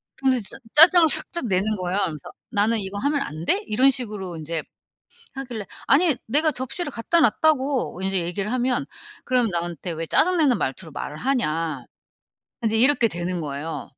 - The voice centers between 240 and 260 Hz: No, high, 220 Hz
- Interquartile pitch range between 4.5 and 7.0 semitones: No, wide, 7.6 semitones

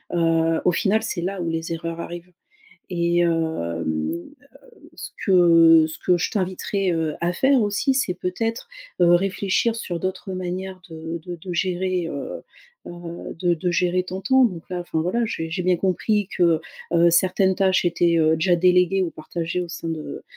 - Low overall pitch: No, medium, 175 Hz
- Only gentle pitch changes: Yes, narrow, 2.1 semitones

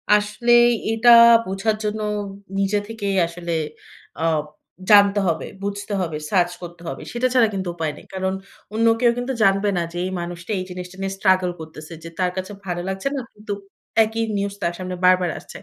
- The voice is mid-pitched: No, high, 195 Hz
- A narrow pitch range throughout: No, average, 3.0 semitones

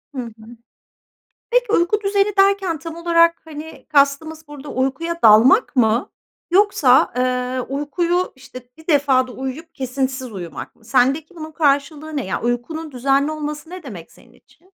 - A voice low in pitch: No, very high, 290 Hz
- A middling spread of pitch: Yes, average, 4.6 semitones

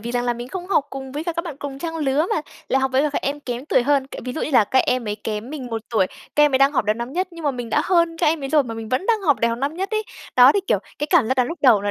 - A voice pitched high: Yes, very high, 270 Hz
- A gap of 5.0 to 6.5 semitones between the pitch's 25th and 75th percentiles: No, average, 4.4 semitones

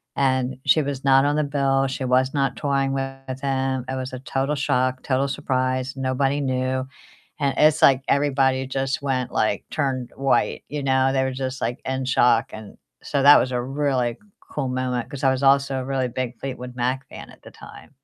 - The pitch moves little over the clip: Yes, narrow, 1.1 semitones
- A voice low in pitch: Yes, low, 130 Hz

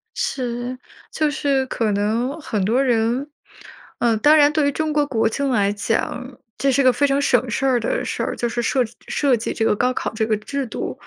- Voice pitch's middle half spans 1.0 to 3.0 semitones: No, average, 3.6 semitones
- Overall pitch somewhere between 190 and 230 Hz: No, very high, 250 Hz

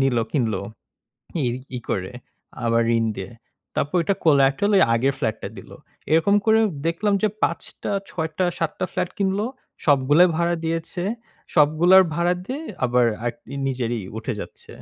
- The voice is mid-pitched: Yes, medium, 160 Hz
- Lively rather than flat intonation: Yes, wide, 6.2 semitones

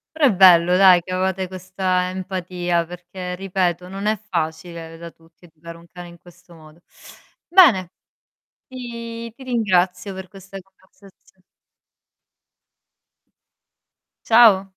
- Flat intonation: Yes, narrow, 1.9 semitones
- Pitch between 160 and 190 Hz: Yes, medium, 185 Hz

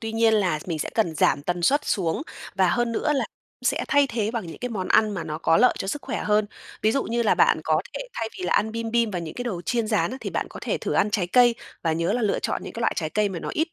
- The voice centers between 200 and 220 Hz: Yes, high, 215 Hz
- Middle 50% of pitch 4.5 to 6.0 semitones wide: Yes, average, 4.8 semitones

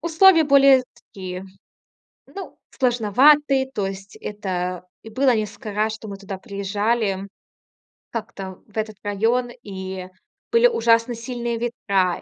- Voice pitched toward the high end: Yes, high, 220 Hz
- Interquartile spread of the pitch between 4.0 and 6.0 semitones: Yes, average, 4.3 semitones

